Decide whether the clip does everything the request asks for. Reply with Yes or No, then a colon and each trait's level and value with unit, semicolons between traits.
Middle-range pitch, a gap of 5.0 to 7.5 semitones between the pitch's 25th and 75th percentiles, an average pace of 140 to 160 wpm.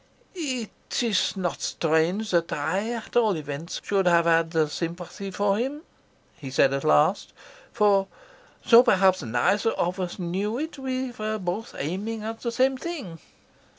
No: high, 195 Hz; wide, 5.4 semitones; average, 150 wpm